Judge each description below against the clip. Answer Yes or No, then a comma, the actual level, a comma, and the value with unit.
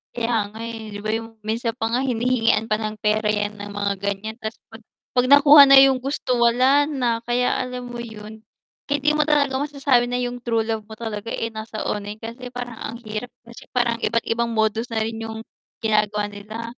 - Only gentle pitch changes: Yes, narrow, 2.3 semitones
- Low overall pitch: No, high, 230 Hz